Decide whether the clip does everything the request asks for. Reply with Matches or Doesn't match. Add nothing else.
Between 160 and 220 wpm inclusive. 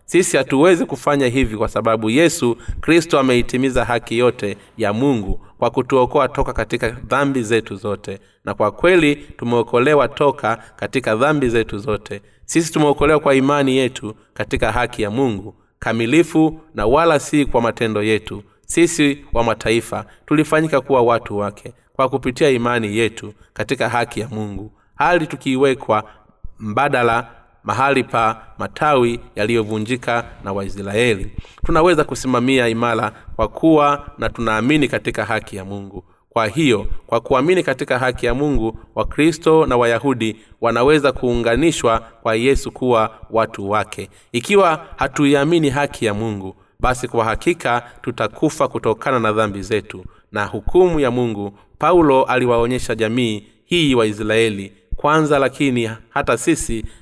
Doesn't match